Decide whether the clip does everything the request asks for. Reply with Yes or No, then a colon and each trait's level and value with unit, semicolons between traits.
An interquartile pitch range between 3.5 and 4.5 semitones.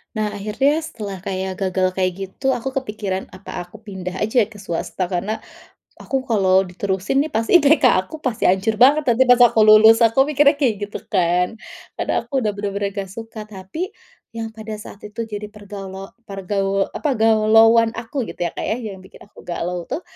No: average, 3.0 semitones